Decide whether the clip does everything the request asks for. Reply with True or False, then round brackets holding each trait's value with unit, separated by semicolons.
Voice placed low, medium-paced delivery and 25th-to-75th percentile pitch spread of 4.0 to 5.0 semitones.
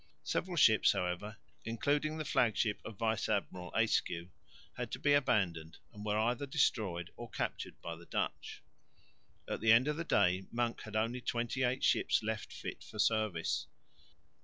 True (110 Hz; 165 wpm; 4.4 semitones)